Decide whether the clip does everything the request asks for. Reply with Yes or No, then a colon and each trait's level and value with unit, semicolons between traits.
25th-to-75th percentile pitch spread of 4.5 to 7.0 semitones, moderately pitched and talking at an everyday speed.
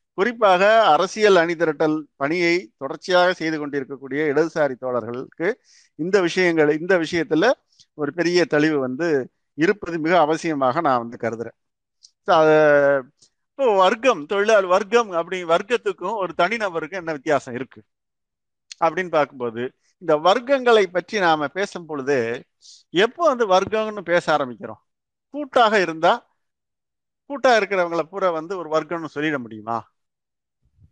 Yes: average, 4.8 semitones; medium, 165 Hz; average, 110 wpm